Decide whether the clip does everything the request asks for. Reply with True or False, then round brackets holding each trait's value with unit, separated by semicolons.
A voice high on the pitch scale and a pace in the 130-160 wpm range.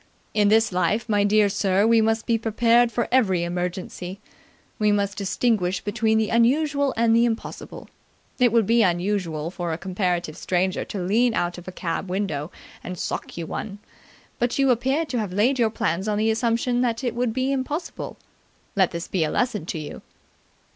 False (210 Hz; 185 wpm)